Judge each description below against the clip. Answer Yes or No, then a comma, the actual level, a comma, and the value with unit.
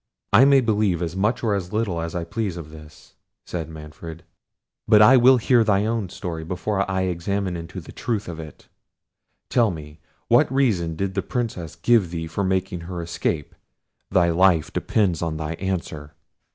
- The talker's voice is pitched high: No, very low, 90 Hz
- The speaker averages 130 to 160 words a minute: No, average, 180 wpm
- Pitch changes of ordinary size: Yes, average, 4.4 semitones